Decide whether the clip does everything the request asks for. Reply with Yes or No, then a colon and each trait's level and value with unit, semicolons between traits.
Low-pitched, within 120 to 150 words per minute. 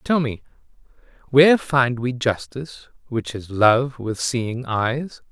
Yes: low, 125 Hz; slow, 135 wpm